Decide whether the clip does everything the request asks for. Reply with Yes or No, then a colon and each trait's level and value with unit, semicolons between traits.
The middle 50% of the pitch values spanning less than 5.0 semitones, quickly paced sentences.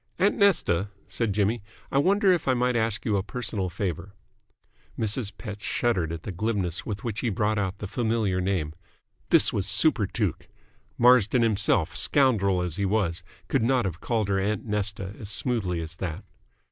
No: average, 3.9 semitones; average, 170 wpm